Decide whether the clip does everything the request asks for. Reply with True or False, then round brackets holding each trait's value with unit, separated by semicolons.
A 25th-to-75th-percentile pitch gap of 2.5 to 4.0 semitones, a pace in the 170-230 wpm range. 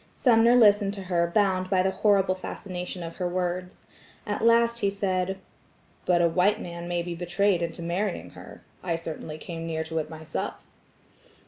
True (2.8 semitones; 175 wpm)